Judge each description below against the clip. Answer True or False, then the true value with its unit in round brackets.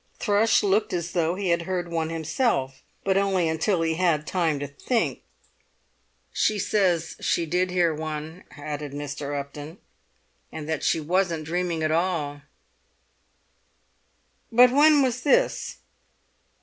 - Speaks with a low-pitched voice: False (170 Hz)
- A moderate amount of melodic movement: True (3.7 semitones)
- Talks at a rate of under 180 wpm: True (135 wpm)